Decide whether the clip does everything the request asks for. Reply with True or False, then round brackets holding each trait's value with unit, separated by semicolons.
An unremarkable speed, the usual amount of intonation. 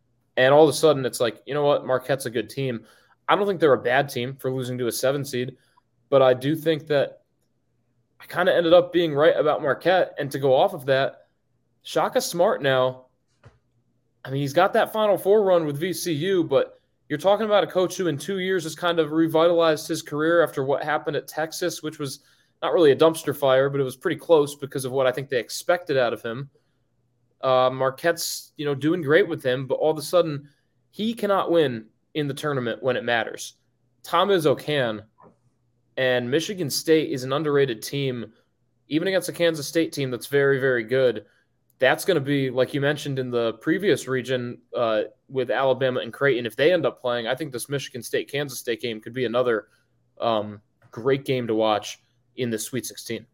False (210 wpm; 4.4 semitones)